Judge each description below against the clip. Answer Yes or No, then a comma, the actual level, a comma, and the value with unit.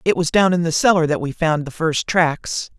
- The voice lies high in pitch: No, medium, 165 Hz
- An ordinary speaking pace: No, fast, 260 wpm